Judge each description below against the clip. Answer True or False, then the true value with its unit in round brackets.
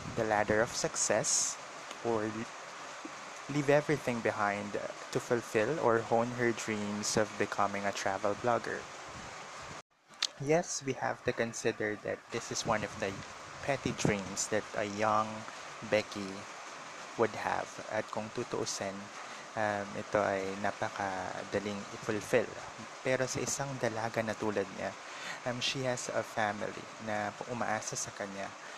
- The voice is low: True (110 Hz)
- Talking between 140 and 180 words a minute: False (130 wpm)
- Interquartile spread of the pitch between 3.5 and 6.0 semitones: False (2.7 semitones)